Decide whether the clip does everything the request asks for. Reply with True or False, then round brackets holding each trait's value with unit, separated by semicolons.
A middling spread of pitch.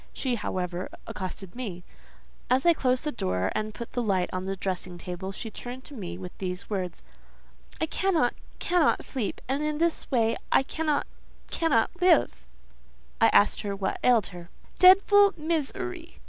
False (8.5 semitones)